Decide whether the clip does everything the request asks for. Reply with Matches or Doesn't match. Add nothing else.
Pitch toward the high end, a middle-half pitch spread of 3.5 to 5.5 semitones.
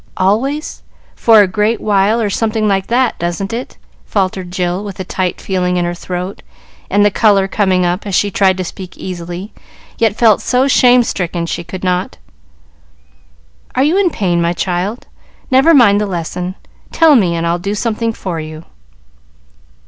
Matches